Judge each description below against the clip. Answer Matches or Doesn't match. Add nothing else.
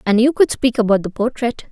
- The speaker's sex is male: Doesn't match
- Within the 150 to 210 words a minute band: Doesn't match